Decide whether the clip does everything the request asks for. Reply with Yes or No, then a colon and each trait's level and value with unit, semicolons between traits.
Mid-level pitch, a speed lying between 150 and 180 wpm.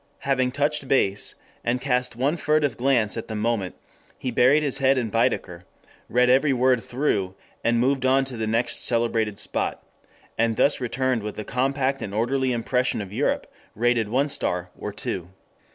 No: low, 125 Hz; average, 170 wpm